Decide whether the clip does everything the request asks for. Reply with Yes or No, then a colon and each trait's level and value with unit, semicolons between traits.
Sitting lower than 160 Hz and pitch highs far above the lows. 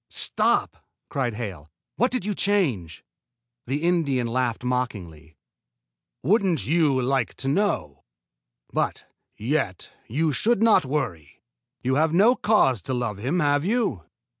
Yes: low, 135 Hz; wide, 7.1 semitones